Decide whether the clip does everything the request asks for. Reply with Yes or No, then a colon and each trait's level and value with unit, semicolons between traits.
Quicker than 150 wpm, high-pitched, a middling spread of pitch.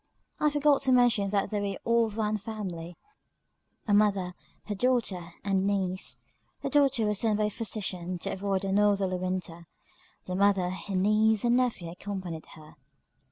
Yes: average, 165 wpm; high, 200 Hz; average, 3.0 semitones